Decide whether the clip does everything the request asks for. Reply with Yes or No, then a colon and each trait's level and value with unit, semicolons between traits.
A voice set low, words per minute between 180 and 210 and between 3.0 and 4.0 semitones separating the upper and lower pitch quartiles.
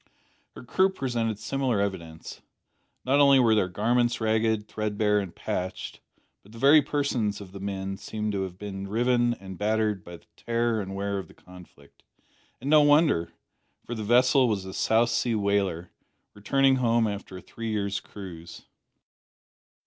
No: low, 110 Hz; average, 165 wpm; average, 3.6 semitones